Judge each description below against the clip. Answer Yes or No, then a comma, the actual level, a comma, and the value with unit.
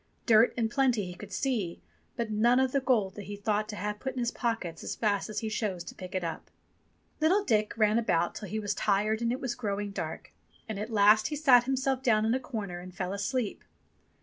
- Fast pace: Yes, fast, 230 wpm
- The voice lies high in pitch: Yes, high, 215 Hz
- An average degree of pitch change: Yes, average, 3.2 semitones